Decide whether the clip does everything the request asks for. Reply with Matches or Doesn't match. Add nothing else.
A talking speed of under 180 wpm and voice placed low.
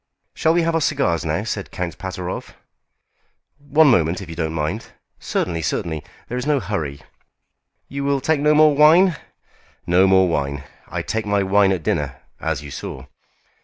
Matches